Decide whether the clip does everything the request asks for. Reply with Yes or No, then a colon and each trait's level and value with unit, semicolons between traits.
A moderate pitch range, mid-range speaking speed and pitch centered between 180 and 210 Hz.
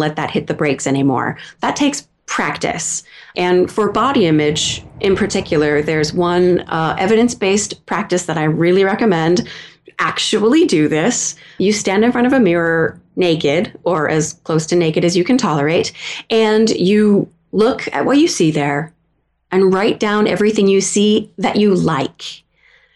Yes: average, 5.0 semitones; average, 160 wpm; medium, 185 Hz